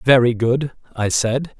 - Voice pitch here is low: Yes, low, 125 Hz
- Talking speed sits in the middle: Yes, average, 150 wpm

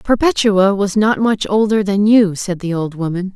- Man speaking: No, female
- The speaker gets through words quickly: No, average, 195 wpm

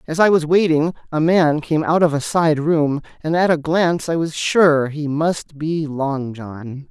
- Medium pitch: Yes, medium, 155 Hz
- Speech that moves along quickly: Yes, fast, 210 wpm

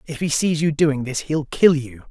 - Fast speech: Yes, fast, 255 wpm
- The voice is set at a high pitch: No, medium, 145 Hz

